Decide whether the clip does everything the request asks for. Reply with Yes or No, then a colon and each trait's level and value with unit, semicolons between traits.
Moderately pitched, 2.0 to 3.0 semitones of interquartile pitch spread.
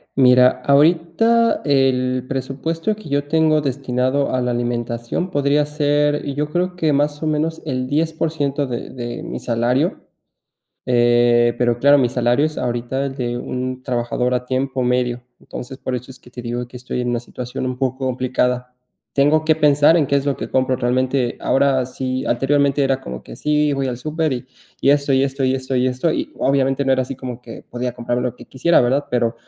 No: low, 130 Hz; average, 2.7 semitones